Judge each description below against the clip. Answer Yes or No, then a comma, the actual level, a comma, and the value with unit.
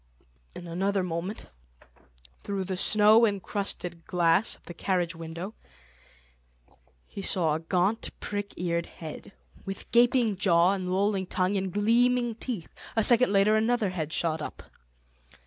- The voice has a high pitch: Yes, high, 195 Hz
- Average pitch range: Yes, average, 3.6 semitones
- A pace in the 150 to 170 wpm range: No, slow, 135 wpm